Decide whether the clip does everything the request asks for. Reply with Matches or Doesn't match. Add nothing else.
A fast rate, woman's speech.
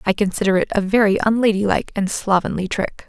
Doesn't match